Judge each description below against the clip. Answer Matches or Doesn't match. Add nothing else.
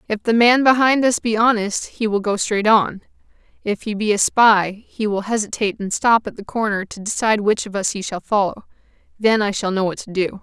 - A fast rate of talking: Matches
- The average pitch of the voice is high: Matches